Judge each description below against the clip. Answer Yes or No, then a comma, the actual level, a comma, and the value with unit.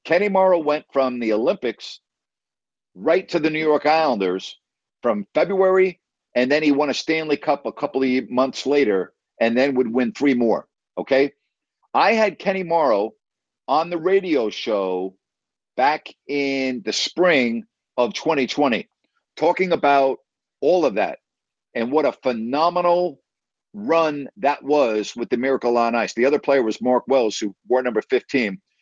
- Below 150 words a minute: No, average, 155 wpm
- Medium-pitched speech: Yes, medium, 145 Hz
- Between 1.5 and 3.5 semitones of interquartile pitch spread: No, average, 5.0 semitones